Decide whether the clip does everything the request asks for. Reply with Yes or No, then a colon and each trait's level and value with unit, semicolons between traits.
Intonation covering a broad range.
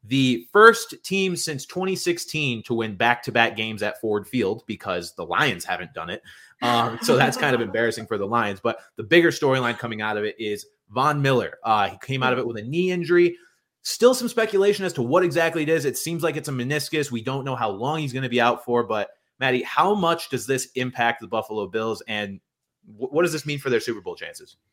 Yes: wide, 6.4 semitones